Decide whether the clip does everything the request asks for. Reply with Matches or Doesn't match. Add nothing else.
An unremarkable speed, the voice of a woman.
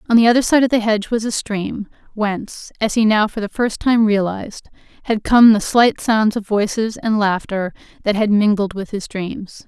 Doesn't match